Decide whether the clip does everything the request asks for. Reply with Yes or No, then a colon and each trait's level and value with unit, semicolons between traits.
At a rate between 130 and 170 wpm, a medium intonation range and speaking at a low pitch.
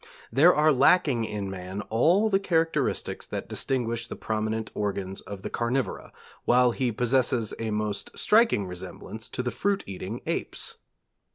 Yes: average, 150 wpm; average, 4.7 semitones; low, 115 Hz